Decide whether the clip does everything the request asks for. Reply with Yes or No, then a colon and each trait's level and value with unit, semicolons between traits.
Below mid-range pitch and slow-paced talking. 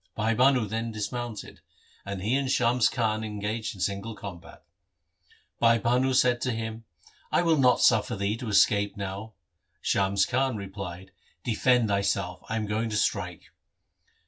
No: low, 110 Hz; average, 160 wpm